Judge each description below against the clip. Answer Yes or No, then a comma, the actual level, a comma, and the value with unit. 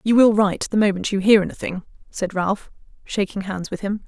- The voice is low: No, high, 200 Hz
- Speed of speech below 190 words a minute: No, fast, 205 wpm